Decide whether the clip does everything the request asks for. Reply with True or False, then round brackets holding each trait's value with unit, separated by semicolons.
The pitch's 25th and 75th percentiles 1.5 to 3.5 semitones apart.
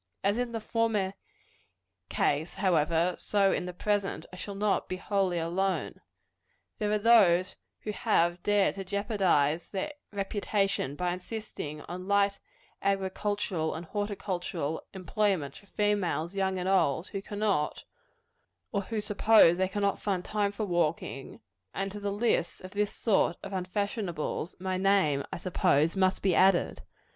True (2.7 semitones)